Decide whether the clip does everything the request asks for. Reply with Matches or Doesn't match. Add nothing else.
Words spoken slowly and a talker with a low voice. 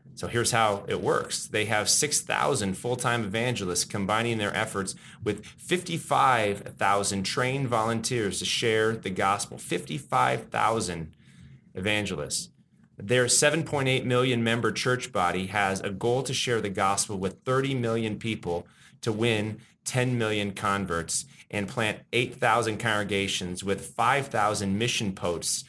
Matches